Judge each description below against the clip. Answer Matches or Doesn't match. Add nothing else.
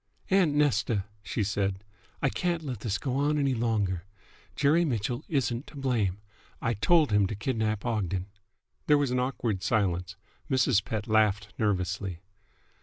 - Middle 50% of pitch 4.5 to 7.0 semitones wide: Matches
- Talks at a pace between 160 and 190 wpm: Doesn't match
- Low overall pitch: Matches